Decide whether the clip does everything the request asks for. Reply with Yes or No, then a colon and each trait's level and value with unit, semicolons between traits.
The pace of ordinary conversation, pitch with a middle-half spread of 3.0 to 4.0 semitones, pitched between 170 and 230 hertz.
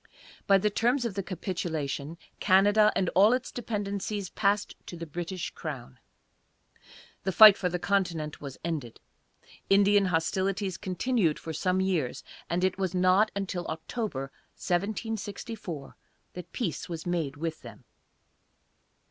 No: slow, 130 wpm; average, 3.5 semitones; medium, 185 Hz